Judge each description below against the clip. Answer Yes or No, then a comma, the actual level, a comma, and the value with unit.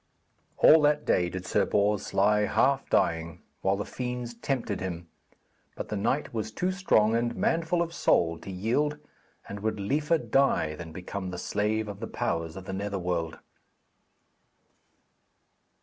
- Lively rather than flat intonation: Yes, wide, 6.4 semitones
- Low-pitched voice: Yes, low, 105 Hz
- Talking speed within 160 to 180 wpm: No, average, 150 wpm